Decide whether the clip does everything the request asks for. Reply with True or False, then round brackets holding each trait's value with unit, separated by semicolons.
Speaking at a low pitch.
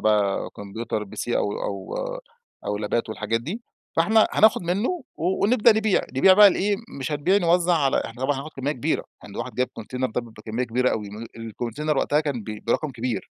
True (130 Hz)